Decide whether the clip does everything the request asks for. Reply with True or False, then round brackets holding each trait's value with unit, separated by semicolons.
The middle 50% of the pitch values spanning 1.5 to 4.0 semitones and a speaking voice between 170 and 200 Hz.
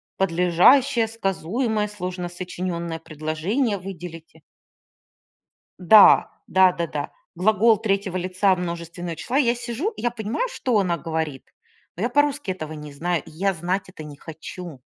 False (4.6 semitones; 185 Hz)